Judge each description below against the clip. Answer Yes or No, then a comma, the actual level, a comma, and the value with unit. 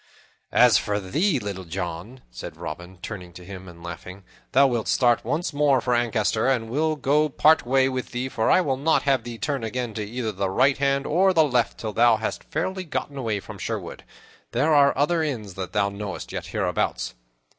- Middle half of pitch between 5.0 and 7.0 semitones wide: Yes, wide, 5.6 semitones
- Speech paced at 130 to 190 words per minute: No, fast, 205 wpm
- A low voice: Yes, low, 120 Hz